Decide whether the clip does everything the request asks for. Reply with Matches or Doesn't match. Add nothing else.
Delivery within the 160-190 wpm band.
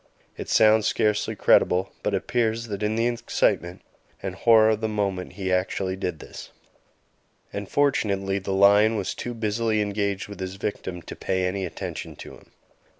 Matches